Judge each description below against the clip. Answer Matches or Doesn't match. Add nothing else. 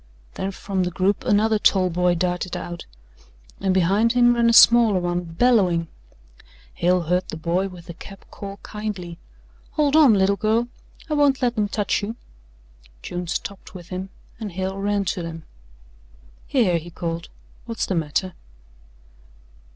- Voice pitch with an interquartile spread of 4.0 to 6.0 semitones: Doesn't match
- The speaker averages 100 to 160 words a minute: Matches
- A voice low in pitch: Doesn't match